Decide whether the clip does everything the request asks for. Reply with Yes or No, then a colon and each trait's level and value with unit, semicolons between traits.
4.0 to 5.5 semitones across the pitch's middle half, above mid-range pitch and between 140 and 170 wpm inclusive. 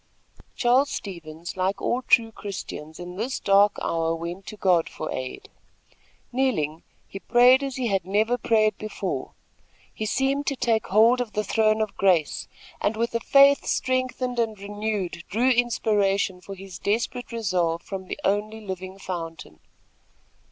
Yes: average, 4.4 semitones; high, 210 Hz; average, 150 wpm